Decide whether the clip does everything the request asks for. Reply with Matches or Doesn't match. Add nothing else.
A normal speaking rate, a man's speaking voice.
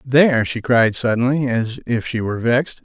Matches